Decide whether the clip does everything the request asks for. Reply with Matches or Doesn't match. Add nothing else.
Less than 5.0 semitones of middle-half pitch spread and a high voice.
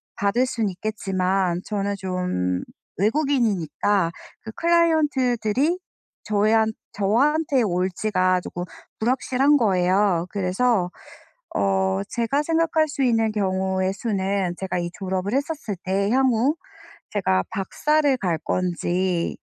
Doesn't match